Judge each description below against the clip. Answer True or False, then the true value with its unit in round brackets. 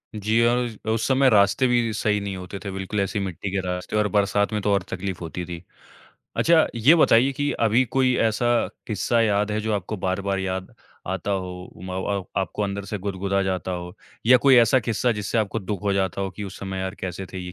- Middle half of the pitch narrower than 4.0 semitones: True (3.0 semitones)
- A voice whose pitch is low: True (100 Hz)